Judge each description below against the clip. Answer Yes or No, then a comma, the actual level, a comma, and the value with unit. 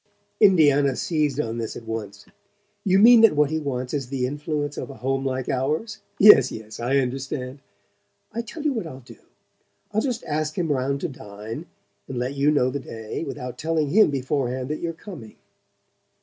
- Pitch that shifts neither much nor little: Yes, average, 4.0 semitones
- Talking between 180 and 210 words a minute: Yes, average, 185 wpm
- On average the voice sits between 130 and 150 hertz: Yes, medium, 140 Hz